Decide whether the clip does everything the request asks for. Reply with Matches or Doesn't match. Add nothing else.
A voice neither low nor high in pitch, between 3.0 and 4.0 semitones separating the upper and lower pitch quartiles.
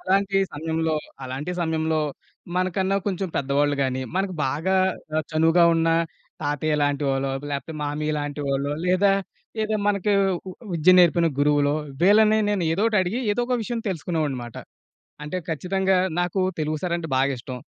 Doesn't match